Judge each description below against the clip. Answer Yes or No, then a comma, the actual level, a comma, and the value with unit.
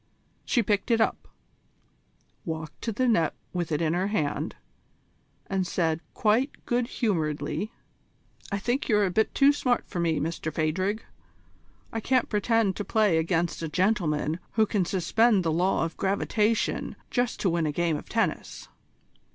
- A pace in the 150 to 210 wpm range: Yes, average, 160 wpm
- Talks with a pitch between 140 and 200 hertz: Yes, high, 190 Hz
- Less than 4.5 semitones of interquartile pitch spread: No, average, 5.1 semitones